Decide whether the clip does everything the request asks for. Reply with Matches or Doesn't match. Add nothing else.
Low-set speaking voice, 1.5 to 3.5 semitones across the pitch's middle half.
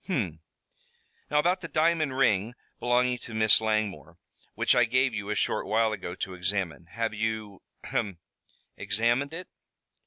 Doesn't match